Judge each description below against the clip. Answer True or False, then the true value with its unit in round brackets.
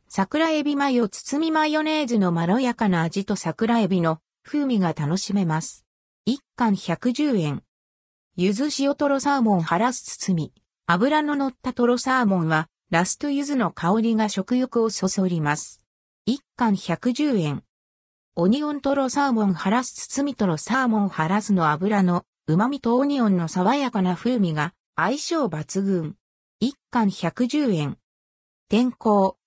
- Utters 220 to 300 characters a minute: True (270 characters per minute)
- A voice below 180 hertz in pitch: False (210 Hz)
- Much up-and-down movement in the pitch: True (7.2 semitones)